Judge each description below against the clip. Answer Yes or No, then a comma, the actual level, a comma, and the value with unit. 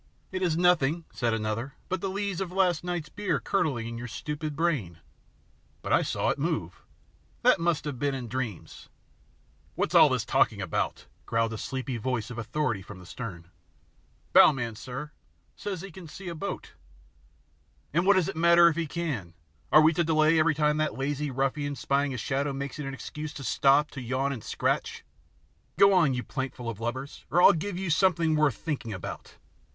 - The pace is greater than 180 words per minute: Yes, average, 195 wpm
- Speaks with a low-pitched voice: No, medium, 145 Hz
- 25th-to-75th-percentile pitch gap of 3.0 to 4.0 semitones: No, average, 5.3 semitones